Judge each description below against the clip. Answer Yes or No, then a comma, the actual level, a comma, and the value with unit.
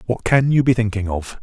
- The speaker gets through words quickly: Yes, fast, 250 wpm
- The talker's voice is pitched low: Yes, low, 115 Hz